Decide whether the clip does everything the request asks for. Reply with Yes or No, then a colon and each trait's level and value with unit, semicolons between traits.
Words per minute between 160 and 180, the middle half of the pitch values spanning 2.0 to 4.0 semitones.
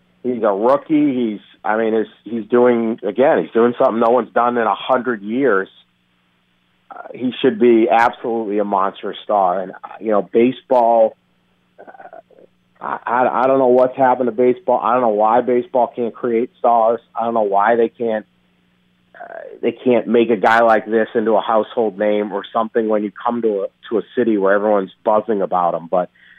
No: average, 190 wpm; average, 3.1 semitones